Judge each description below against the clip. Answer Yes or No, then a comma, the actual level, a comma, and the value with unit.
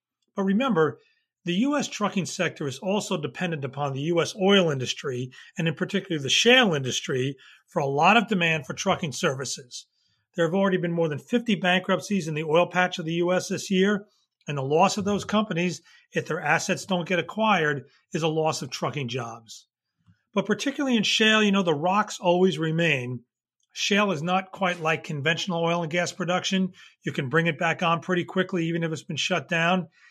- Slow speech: No, average, 195 wpm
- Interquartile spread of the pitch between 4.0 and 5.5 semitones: No, average, 3.5 semitones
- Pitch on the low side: No, medium, 175 Hz